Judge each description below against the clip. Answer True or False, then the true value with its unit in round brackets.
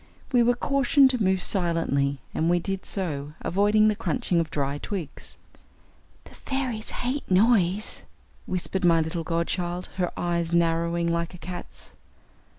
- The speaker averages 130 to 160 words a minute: True (145 wpm)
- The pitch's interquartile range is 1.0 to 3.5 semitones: False (4.1 semitones)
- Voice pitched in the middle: True (180 Hz)